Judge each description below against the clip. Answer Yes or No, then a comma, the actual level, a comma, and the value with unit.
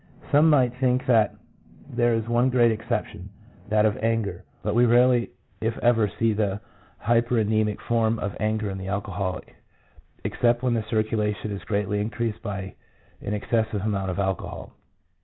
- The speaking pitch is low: Yes, low, 110 Hz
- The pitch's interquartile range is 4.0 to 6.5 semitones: No, narrow, 2.4 semitones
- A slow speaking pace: No, average, 155 wpm